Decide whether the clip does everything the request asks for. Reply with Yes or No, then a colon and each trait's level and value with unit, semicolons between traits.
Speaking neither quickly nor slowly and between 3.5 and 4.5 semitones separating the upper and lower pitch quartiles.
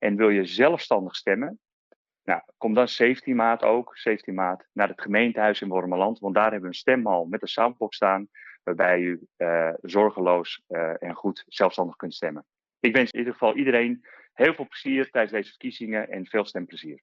Yes: average, 185 wpm; average, 4.2 semitones